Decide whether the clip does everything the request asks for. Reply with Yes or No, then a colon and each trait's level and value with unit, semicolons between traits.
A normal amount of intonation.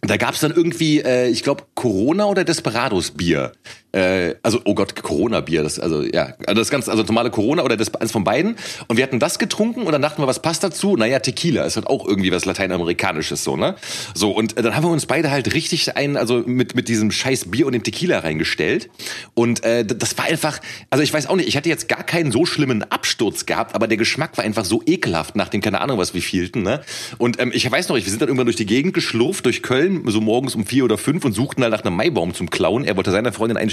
No: wide, 5.7 semitones